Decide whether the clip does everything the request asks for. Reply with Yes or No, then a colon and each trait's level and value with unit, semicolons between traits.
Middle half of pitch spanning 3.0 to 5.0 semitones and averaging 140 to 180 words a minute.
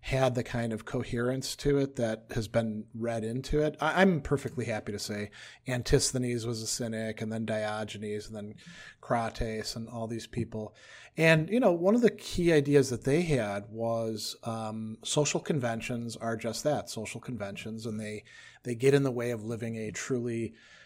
Yes: average, 3.3 semitones; average, 175 wpm